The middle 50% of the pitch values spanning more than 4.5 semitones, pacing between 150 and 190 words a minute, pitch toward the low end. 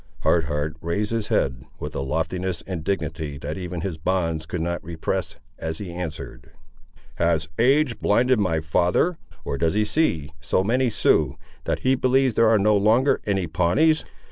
Yes: average, 5.3 semitones; average, 170 wpm; very low, 90 Hz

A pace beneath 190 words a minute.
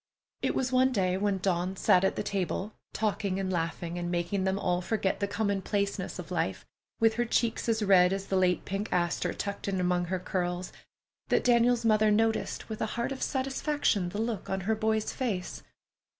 No: average, 195 wpm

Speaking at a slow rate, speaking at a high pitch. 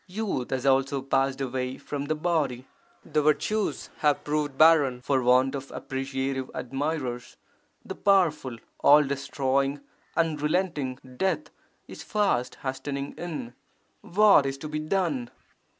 No: slow, 125 wpm; medium, 140 Hz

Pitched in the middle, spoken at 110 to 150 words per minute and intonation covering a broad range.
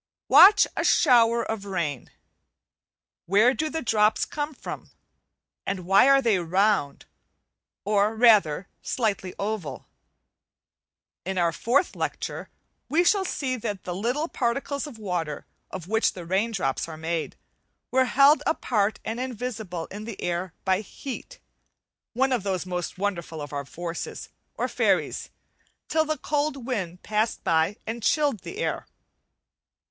No: high, 215 Hz; average, 140 wpm; wide, 6.1 semitones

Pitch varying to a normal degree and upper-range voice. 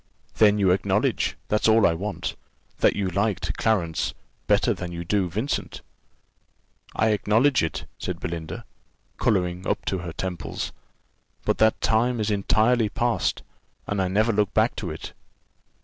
No: average, 3.5 semitones; low, 100 Hz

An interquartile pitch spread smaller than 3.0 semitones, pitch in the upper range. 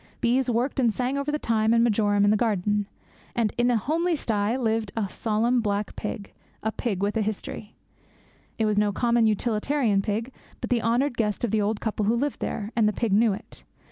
Yes: narrow, 2.4 semitones; high, 220 Hz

